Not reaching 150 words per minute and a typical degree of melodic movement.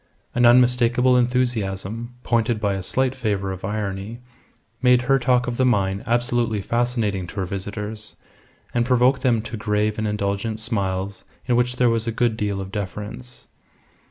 No: average, 160 wpm; average, 3.3 semitones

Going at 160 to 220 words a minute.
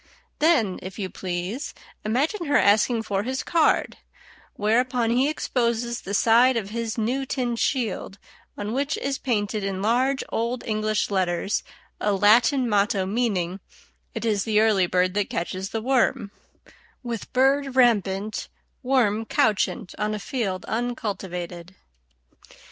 No: slow, 135 wpm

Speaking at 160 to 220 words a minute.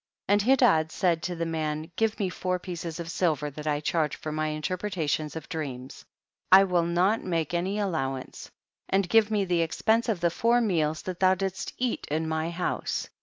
Yes: average, 200 wpm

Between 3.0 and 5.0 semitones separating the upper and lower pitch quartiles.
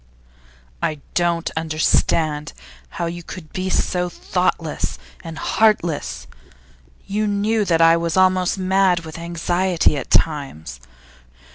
No: narrow, 2.6 semitones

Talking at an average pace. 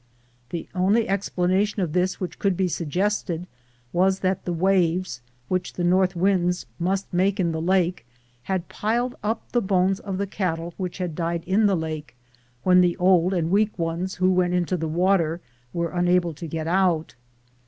Yes: average, 175 wpm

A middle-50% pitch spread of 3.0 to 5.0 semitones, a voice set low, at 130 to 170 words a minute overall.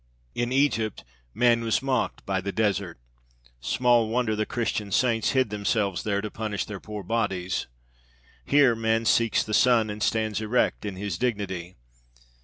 No: narrow, 2.6 semitones; low, 110 Hz; average, 155 wpm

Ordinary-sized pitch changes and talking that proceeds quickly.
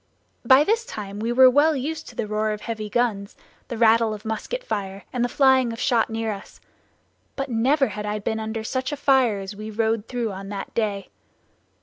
Yes: average, 3.5 semitones; fast, 210 wpm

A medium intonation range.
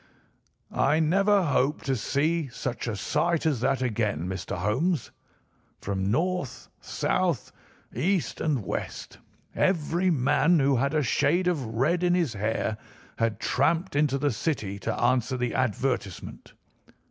No: wide, 6.2 semitones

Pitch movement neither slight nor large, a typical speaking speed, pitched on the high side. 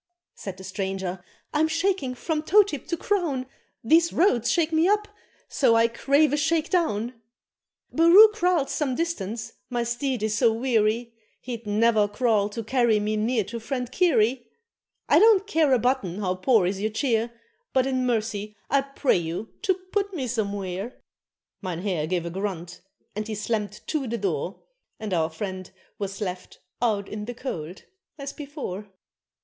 No: wide, 5.7 semitones; average, 165 wpm; high, 230 Hz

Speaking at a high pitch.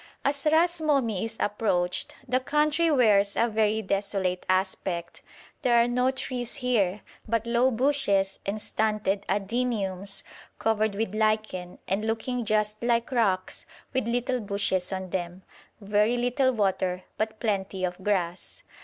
Yes: high, 215 Hz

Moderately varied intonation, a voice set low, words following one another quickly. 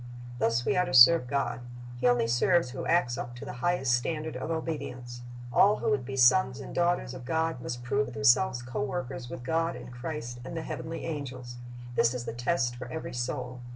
Yes: average, 4.7 semitones; low, 130 Hz; fast, 210 wpm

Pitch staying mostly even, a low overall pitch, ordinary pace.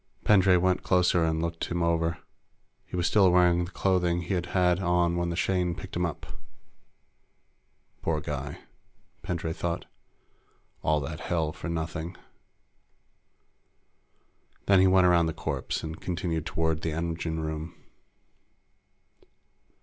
No: narrow, 1.7 semitones; very low, 85 Hz; slow, 130 wpm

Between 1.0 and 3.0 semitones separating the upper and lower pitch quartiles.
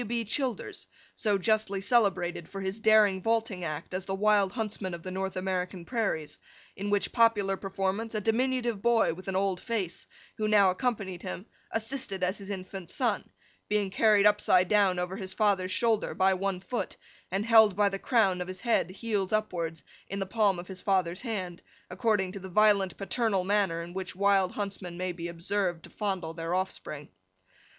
Yes: narrow, 2.6 semitones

